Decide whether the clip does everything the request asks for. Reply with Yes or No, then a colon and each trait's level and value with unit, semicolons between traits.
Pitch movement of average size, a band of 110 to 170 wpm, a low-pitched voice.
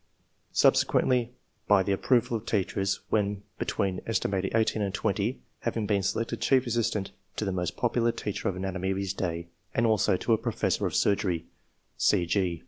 Yes: average, 3.0 semitones; average, 160 wpm; low, 105 Hz